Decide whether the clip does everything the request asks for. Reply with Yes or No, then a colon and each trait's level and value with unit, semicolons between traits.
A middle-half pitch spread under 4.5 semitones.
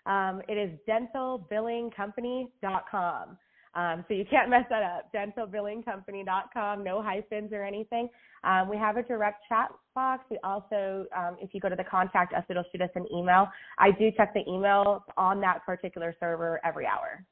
Yes: average, 2.9 semitones